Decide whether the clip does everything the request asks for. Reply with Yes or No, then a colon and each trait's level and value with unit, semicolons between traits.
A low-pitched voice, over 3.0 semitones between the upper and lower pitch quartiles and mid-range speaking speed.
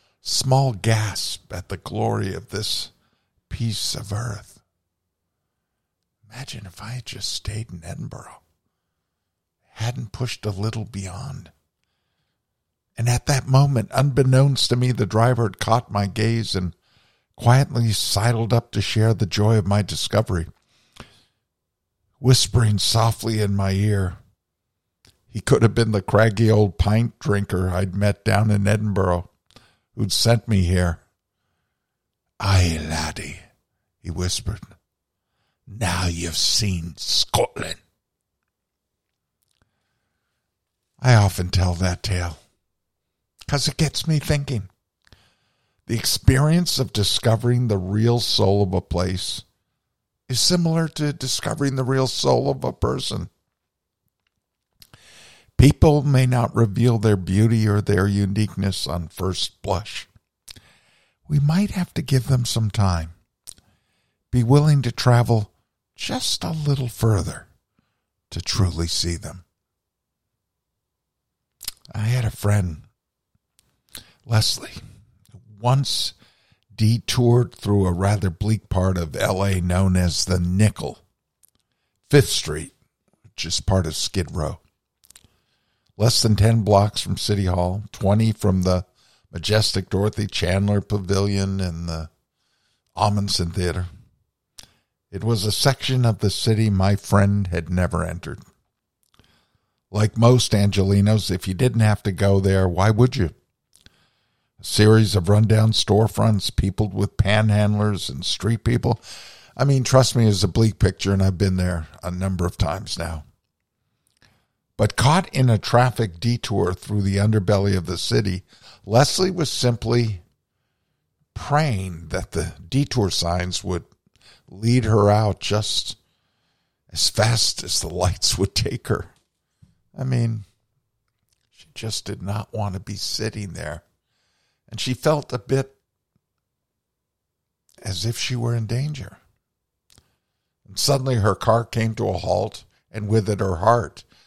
No: low, 105 Hz; average, 3.9 semitones; slow, 125 wpm